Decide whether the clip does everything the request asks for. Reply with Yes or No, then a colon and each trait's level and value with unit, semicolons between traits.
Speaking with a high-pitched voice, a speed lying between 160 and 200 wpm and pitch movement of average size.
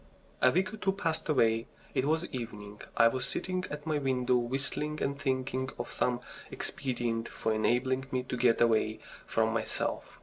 No: low, 130 Hz; average, 170 wpm; average, 3.8 semitones